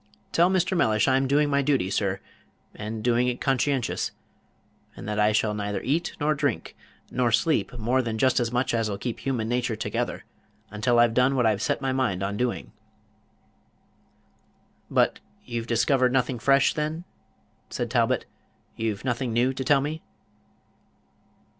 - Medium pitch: No, low, 125 Hz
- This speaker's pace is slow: No, average, 155 wpm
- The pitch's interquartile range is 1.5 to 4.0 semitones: Yes, average, 3.5 semitones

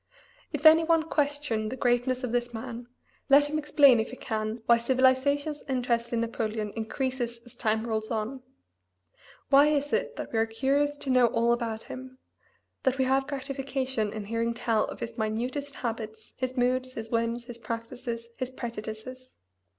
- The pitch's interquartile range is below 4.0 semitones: Yes, average, 2.8 semitones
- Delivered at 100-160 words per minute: No, average, 170 wpm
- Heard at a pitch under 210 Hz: No, high, 245 Hz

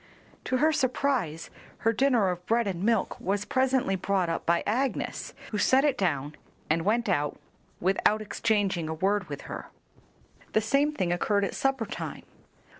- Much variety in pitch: Yes, wide, 6.0 semitones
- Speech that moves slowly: No, average, 165 wpm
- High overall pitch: Yes, high, 205 Hz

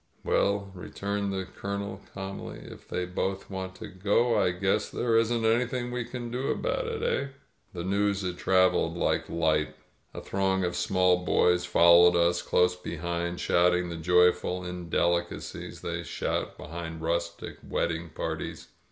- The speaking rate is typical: Yes, average, 150 wpm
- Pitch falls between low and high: No, very low, 90 Hz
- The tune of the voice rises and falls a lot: No, narrow, 2.4 semitones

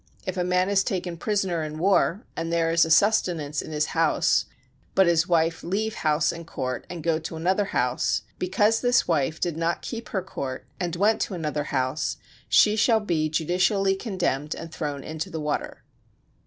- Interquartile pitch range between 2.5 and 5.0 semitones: Yes, average, 3.5 semitones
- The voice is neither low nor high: Yes, medium, 170 Hz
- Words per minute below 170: No, average, 185 wpm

